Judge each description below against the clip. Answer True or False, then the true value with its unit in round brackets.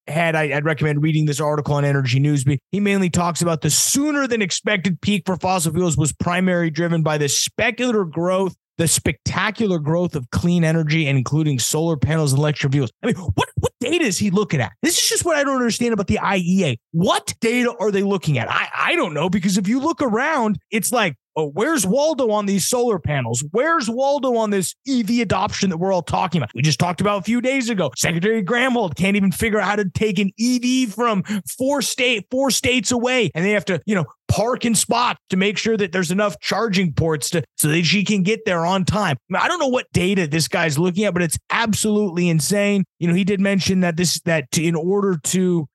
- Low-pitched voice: False (190 Hz)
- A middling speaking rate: False (225 wpm)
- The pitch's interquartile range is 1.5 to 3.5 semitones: False (5.4 semitones)